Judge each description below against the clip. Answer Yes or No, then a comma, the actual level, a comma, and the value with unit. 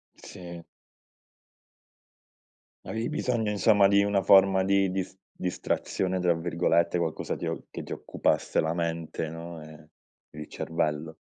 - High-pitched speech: No, very low, 90 Hz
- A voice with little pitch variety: No, average, 3.0 semitones